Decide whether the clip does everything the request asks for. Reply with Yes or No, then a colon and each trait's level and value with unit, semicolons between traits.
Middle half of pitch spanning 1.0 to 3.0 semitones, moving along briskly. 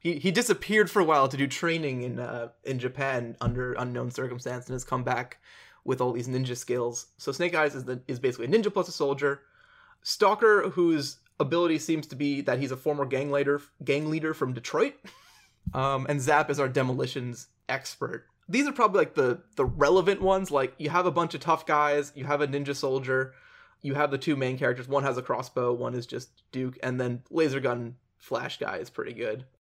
No: average, 3.6 semitones; fast, 210 wpm